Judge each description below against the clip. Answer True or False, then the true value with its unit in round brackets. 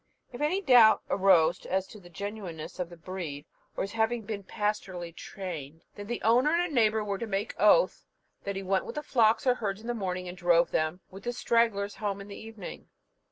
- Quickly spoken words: True (215 wpm)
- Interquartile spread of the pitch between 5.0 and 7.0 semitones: False (3.7 semitones)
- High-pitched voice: True (200 Hz)